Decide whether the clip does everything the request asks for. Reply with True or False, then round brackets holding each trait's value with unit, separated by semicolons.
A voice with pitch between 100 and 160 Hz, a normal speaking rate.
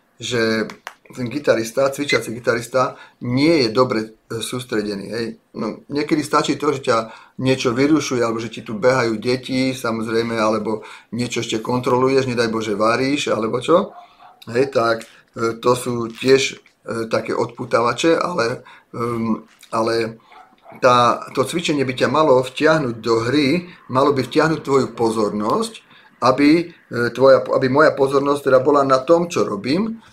True (125 Hz; 125 wpm)